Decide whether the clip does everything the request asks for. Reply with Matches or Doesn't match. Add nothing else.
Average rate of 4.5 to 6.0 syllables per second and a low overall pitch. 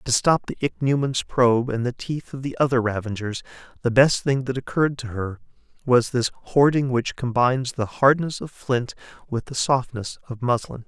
Matches